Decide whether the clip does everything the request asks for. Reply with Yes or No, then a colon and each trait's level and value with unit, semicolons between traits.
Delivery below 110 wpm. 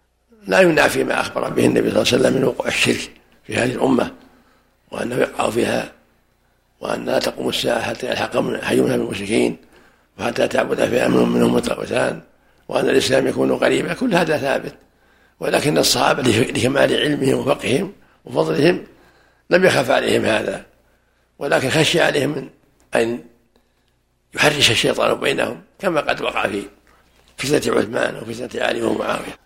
No: fast, 135 wpm